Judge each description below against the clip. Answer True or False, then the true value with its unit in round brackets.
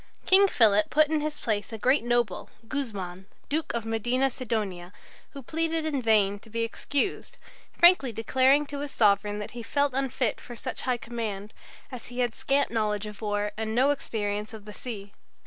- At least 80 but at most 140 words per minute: False (180 wpm)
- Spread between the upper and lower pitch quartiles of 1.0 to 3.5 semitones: False (4.7 semitones)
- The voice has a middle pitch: False (230 Hz)